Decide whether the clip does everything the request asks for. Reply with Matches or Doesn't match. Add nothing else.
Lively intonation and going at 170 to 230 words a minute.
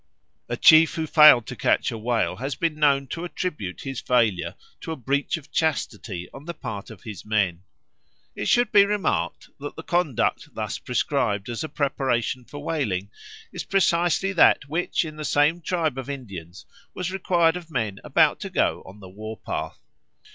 Matches